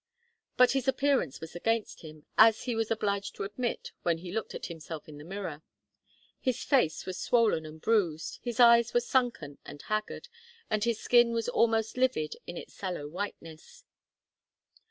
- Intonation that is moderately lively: No, wide, 6.4 semitones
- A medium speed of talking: Yes, average, 170 wpm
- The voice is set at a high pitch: Yes, high, 215 Hz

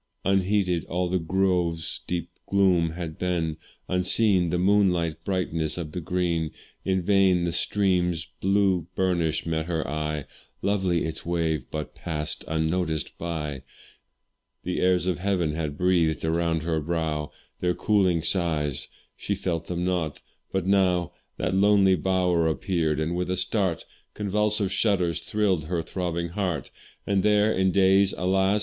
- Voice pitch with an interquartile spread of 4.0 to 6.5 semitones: No, average, 2.7 semitones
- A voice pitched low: Yes, very low, 90 Hz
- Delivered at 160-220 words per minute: No, average, 145 wpm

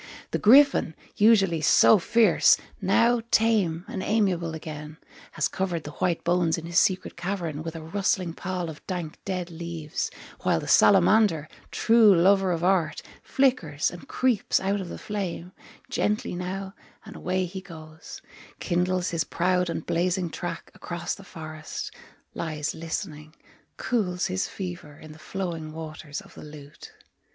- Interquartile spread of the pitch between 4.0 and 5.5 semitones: No, average, 3.2 semitones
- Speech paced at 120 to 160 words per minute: Yes, average, 150 wpm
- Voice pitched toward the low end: No, medium, 175 Hz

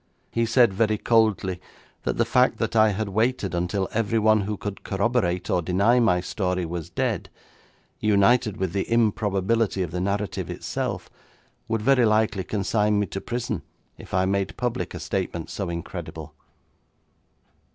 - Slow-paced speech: No, average, 150 wpm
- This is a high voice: No, low, 105 Hz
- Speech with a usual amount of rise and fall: Yes, average, 3.1 semitones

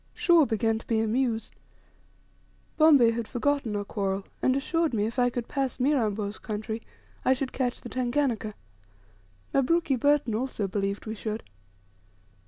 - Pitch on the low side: No, high, 235 Hz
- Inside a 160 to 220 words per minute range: No, average, 145 wpm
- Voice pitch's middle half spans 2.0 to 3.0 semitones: No, average, 3.7 semitones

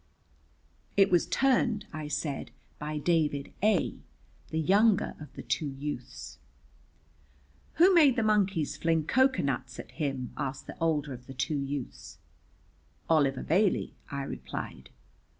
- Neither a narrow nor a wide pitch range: No, wide, 6.3 semitones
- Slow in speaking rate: Yes, slow, 130 wpm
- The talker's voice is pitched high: No, medium, 155 Hz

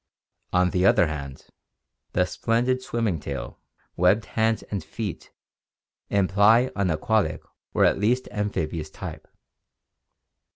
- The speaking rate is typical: No, slow, 115 wpm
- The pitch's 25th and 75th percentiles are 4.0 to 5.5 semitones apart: Yes, average, 4.9 semitones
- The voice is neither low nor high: No, low, 100 Hz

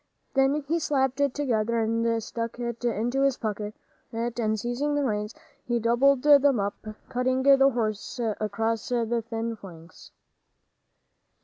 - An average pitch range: Yes, average, 3.4 semitones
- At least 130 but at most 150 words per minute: Yes, slow, 135 wpm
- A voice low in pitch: No, high, 235 Hz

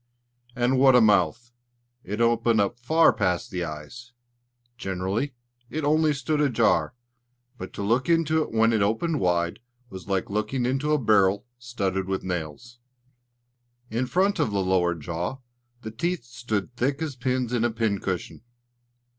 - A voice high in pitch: No, low, 115 Hz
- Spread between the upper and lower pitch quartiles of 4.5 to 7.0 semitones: Yes, average, 5.2 semitones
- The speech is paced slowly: No, average, 155 wpm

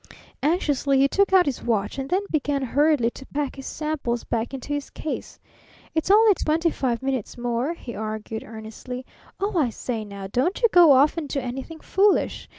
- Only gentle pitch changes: No, average, 5.0 semitones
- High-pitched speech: Yes, very high, 275 Hz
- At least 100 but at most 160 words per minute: No, average, 185 wpm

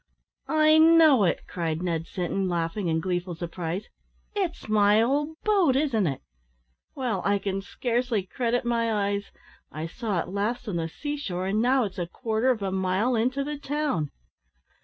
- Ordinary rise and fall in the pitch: No, wide, 6.2 semitones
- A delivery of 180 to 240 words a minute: No, average, 170 wpm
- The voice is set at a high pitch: Yes, high, 210 Hz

